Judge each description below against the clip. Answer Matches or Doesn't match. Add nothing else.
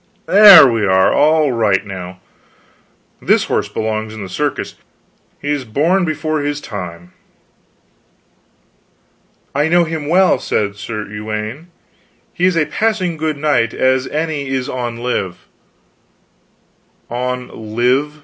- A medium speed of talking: Doesn't match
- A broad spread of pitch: Matches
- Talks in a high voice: Doesn't match